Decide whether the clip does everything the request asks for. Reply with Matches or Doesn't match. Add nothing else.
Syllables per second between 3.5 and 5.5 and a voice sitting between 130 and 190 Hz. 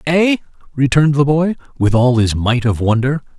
Matches